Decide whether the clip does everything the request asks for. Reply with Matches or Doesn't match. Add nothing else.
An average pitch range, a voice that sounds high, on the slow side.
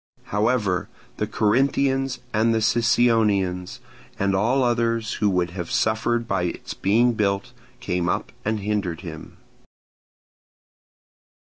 Doesn't match